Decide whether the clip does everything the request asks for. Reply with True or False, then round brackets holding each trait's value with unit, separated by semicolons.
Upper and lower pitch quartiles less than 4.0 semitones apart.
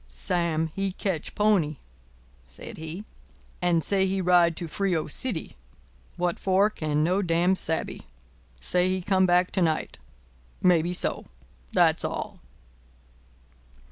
True (2.8 semitones)